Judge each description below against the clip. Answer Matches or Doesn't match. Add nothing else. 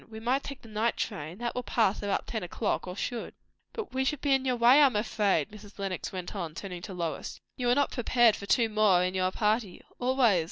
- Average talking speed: Doesn't match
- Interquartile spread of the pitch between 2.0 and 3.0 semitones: Doesn't match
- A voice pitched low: Doesn't match